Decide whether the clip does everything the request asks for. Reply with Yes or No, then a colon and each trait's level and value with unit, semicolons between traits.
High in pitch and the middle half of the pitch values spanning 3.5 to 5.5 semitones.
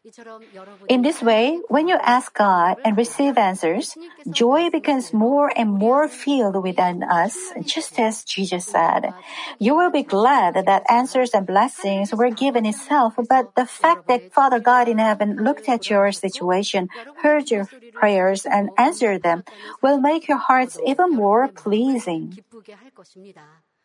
Yes: high, 235 Hz; average, 5.1 semitones